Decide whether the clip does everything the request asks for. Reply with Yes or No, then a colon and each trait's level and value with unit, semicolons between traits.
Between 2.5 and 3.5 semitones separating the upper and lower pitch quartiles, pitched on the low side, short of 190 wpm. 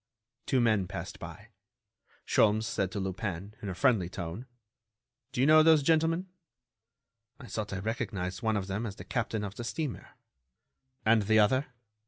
No: average, 4.5 semitones; low, 110 Hz; average, 165 wpm